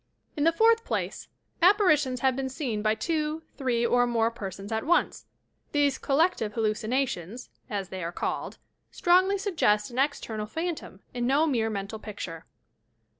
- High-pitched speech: Yes, very high, 255 Hz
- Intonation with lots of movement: Yes, wide, 6.3 semitones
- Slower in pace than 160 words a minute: Yes, average, 150 wpm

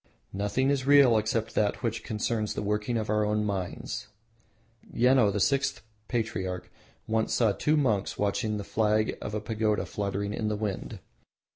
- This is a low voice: Yes, low, 110 Hz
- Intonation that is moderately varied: No, narrow, 1.9 semitones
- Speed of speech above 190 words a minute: No, average, 160 wpm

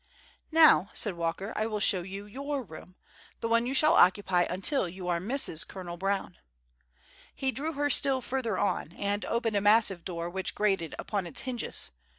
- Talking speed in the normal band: Yes, average, 165 wpm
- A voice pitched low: No, high, 205 Hz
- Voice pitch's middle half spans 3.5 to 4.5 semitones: No, wide, 5.5 semitones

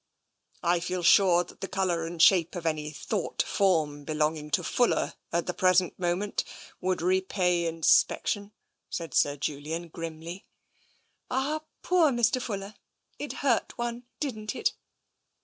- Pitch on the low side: No, medium, 180 Hz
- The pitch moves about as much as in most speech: Yes, average, 3.7 semitones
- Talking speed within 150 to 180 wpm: No, average, 140 wpm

